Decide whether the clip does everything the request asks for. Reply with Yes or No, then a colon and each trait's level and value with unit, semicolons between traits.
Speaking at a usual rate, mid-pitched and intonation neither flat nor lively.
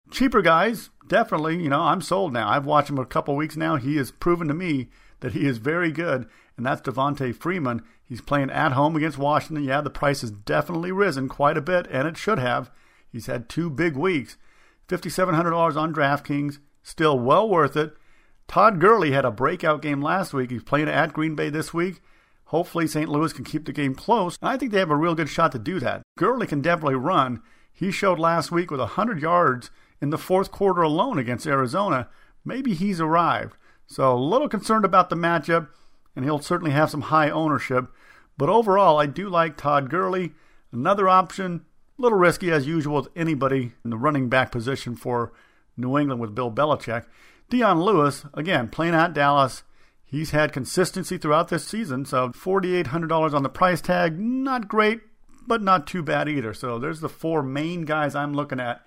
Yes: average, 195 wpm; medium, 155 Hz; average, 3.8 semitones